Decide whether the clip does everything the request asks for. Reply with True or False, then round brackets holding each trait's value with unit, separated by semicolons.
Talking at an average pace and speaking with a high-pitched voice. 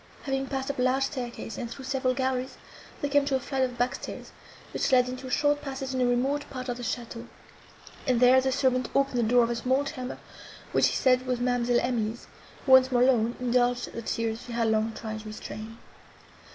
False (220 wpm; 250 Hz)